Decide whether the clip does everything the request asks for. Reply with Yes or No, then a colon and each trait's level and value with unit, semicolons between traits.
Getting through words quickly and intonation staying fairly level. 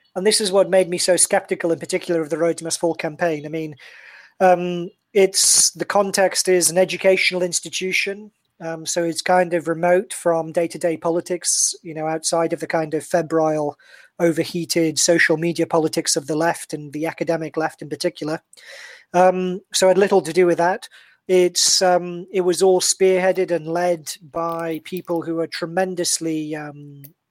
No: average, 170 wpm; narrow, 2.1 semitones